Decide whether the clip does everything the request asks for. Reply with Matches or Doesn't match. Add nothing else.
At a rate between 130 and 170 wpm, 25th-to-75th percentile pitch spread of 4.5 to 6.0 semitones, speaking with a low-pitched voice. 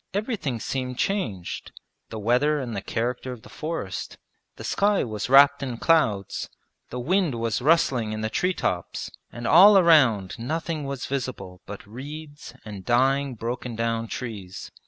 Matches